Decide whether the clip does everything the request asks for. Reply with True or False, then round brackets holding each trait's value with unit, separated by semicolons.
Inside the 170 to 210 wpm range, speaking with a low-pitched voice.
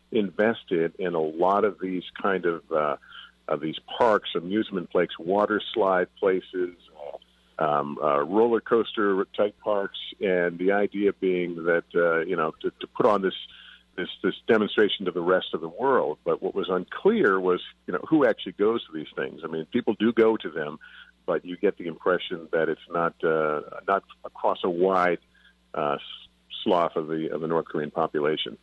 True (180 wpm; 95 Hz)